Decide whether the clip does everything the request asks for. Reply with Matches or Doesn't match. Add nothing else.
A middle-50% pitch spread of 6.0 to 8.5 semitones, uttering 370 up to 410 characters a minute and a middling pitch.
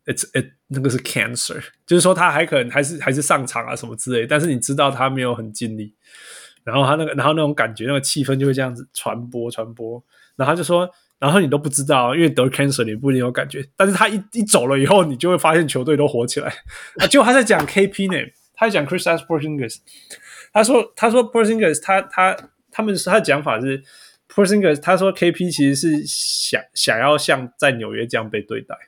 Doesn't match